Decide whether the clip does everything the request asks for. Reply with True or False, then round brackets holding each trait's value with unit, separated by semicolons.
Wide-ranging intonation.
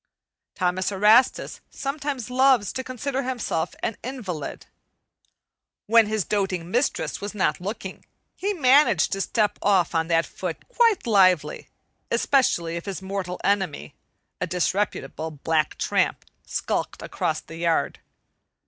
True (6.1 semitones)